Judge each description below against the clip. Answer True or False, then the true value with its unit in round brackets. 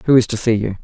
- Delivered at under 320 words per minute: False (360 wpm)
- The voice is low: True (115 Hz)